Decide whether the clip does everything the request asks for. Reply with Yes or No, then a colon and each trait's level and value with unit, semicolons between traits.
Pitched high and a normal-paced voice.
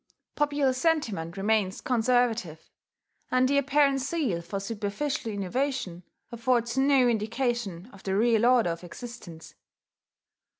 No: high, 235 Hz; slow, 115 wpm